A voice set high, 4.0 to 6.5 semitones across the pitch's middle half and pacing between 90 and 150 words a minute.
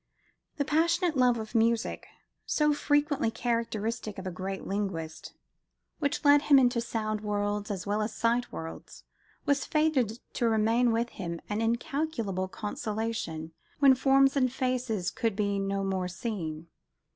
Yes: high, 225 Hz; average, 4.5 semitones; average, 145 wpm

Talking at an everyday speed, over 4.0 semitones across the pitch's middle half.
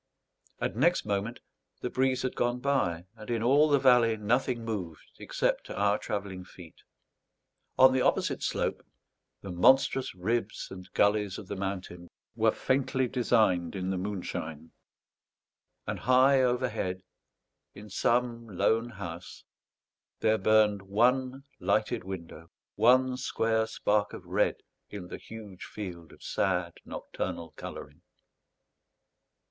No: slow, 125 wpm; average, 4.9 semitones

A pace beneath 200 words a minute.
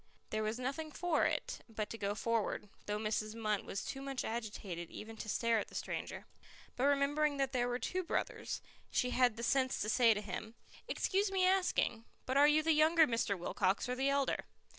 No: fast, 205 wpm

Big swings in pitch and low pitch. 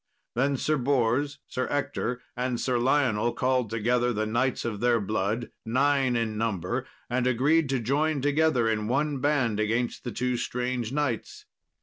No: average, 3.0 semitones; low, 125 Hz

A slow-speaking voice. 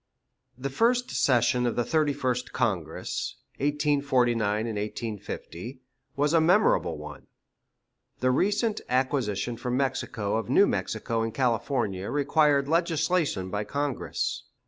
Yes: slow, 115 wpm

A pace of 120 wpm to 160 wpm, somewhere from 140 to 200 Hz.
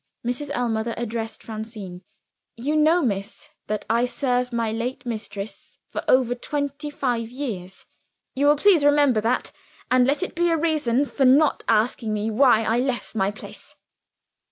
No: average, 155 wpm; high, 245 Hz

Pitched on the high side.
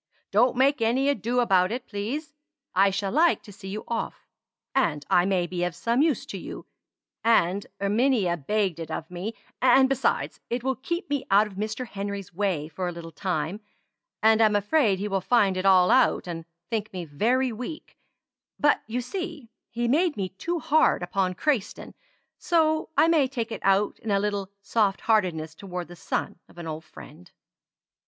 Yes: high, 210 Hz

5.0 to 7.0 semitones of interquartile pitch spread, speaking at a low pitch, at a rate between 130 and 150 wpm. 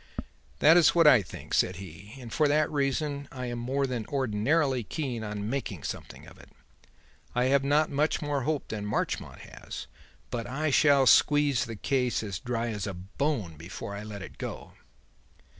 No: average, 5.3 semitones; low, 125 Hz; average, 175 wpm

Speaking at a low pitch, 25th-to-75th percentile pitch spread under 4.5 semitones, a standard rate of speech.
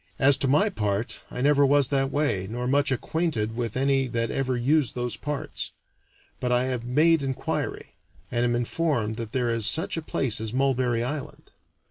Yes: low, 130 Hz; average, 3.2 semitones; average, 180 wpm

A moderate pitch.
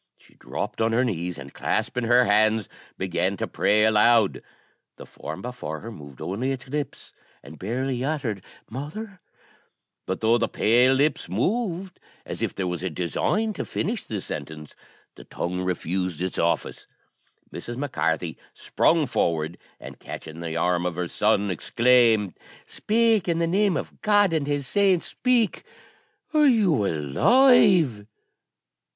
No: low, 115 Hz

